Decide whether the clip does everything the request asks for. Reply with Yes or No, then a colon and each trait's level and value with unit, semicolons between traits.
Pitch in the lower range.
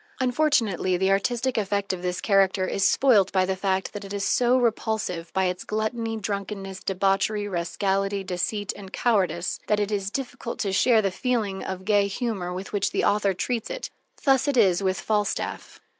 No: high, 200 Hz